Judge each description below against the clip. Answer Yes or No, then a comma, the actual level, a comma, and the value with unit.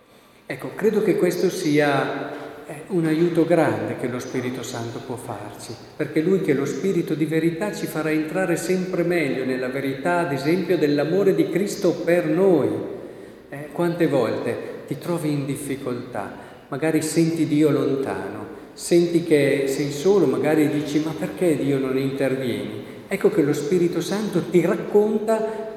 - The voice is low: No, medium, 155 Hz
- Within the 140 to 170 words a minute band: Yes, average, 155 wpm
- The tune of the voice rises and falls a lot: No, average, 3.9 semitones